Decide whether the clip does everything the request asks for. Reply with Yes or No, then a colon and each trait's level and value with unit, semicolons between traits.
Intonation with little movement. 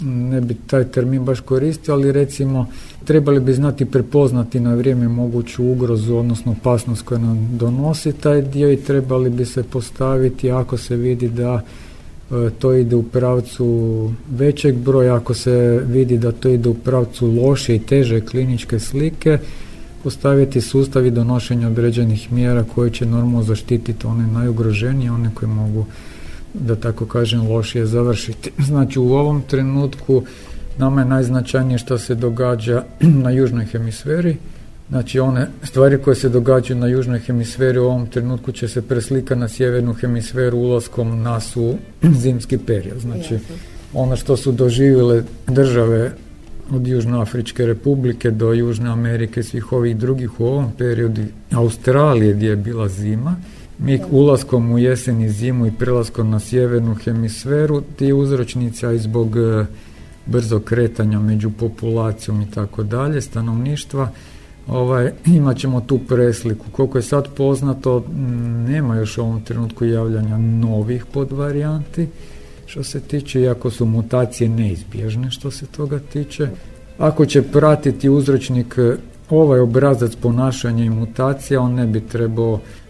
Yes: narrow, 2.3 semitones